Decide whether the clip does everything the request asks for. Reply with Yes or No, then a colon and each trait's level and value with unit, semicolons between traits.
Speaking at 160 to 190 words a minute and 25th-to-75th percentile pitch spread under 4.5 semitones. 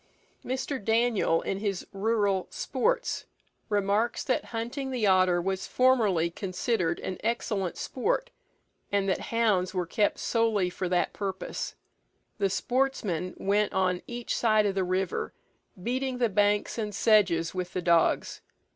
No: average, 140 wpm; average, 3.8 semitones